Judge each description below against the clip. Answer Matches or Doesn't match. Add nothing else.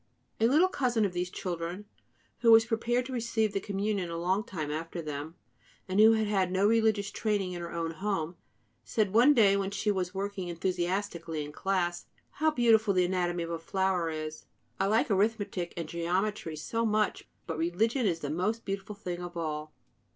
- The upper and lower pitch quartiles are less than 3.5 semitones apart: Doesn't match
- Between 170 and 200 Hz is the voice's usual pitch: Matches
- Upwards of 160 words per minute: Matches